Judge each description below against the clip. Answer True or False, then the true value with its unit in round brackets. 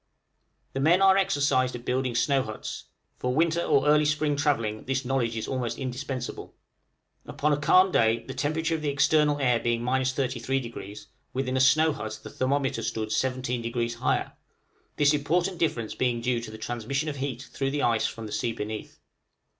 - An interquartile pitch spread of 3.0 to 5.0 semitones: True (3.7 semitones)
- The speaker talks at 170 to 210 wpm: True (175 wpm)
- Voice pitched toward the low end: True (130 Hz)